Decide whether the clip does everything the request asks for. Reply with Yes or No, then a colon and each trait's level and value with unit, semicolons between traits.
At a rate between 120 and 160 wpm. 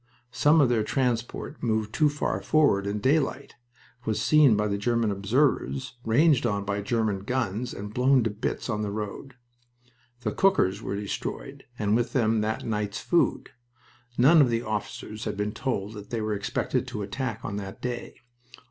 No: average, 170 wpm